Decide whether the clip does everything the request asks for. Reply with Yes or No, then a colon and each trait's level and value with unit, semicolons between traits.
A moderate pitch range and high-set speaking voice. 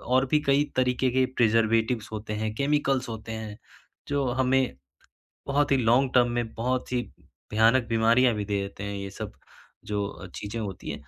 No: average, 3.3 semitones; low, 115 Hz